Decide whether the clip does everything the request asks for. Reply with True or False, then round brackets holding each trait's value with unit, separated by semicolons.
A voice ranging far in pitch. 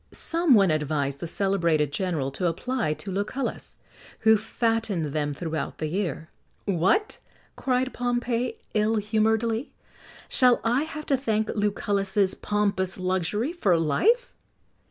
True (6.0 semitones)